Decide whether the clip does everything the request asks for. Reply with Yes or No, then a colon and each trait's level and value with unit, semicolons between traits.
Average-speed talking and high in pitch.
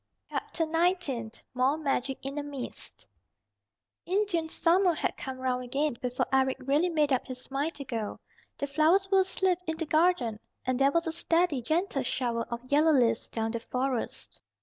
Yes: average, 170 wpm; very high, 280 Hz